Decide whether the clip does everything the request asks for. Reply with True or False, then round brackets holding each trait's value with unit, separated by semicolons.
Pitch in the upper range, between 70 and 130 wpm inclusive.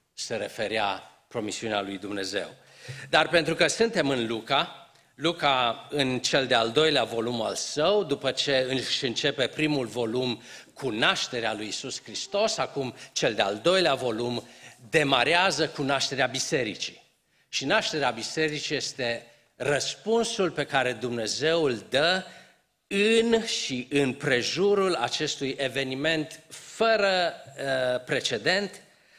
False (140 Hz; 120 wpm)